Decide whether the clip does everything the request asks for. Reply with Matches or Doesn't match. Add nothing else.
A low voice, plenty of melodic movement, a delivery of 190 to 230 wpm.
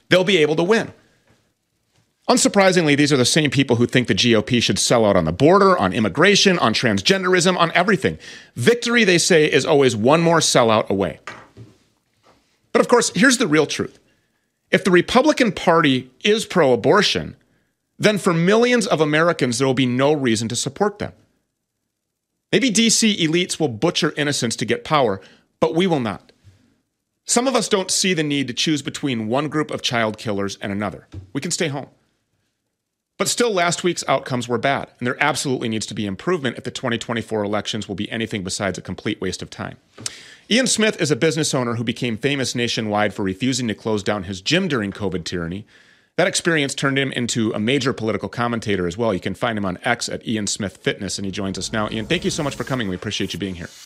Matches